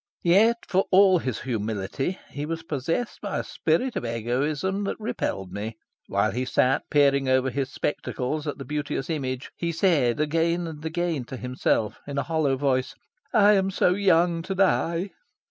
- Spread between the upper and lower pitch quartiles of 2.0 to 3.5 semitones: No, average, 5.2 semitones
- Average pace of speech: Yes, average, 170 wpm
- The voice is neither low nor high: Yes, medium, 150 Hz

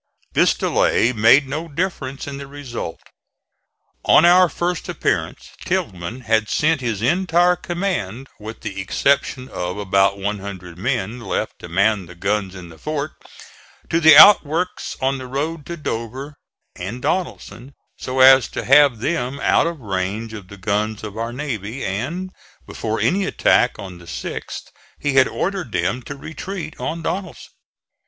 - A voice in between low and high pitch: No, low, 125 Hz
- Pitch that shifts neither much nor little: No, wide, 7.0 semitones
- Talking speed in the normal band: Yes, average, 155 wpm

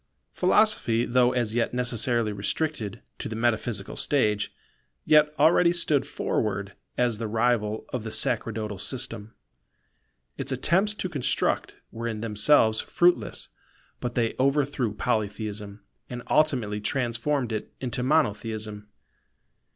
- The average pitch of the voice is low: Yes, low, 120 Hz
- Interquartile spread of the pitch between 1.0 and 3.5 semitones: No, average, 4.1 semitones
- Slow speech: Yes, slow, 120 wpm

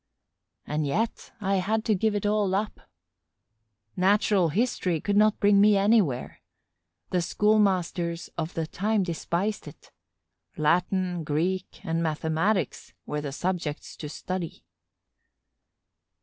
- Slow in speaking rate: Yes, slow, 120 wpm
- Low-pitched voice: No, medium, 185 Hz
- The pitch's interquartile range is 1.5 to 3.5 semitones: No, average, 4.0 semitones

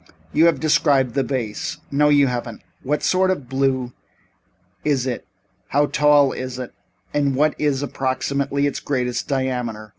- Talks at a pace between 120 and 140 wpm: No, average, 150 wpm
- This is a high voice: No, low, 135 Hz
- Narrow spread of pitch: Yes, narrow, 2.3 semitones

